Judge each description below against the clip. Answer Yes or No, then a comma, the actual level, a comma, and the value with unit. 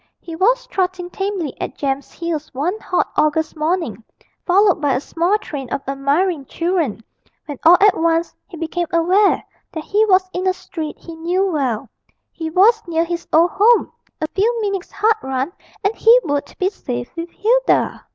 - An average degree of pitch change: Yes, average, 4.2 semitones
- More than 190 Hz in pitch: Yes, very high, 340 Hz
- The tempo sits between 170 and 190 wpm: Yes, average, 175 wpm